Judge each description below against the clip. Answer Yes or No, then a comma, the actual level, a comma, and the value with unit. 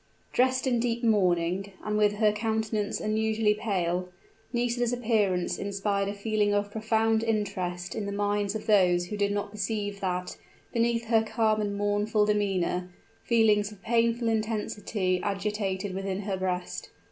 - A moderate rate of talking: Yes, average, 145 wpm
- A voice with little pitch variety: Yes, narrow, 2.1 semitones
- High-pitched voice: Yes, high, 210 Hz